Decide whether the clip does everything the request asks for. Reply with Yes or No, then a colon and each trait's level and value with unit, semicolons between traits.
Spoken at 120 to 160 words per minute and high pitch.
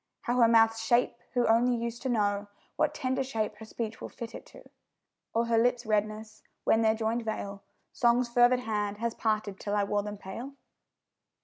No: average, 190 wpm; high, 225 Hz